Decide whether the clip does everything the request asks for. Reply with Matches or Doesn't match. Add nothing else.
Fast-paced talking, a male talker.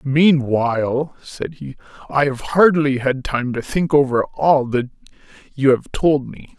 Doesn't match